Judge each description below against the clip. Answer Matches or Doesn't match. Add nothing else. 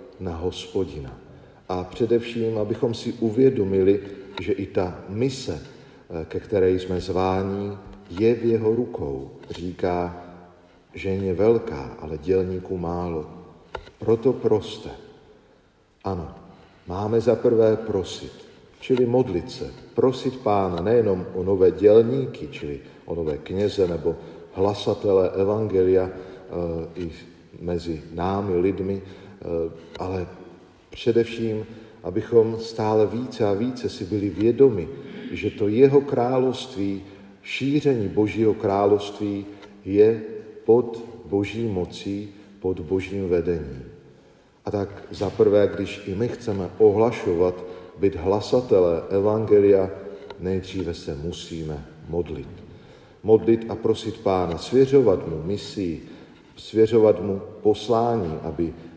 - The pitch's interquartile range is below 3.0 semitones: Doesn't match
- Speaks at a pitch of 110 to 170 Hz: Doesn't match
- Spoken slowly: Matches